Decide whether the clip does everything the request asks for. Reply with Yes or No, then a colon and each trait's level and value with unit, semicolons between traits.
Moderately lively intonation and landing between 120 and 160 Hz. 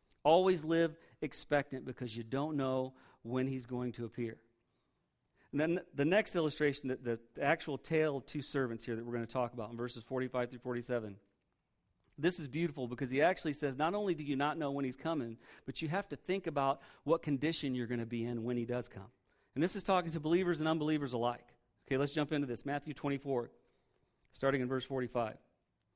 Yes: average, 3.9 semitones; low, 135 Hz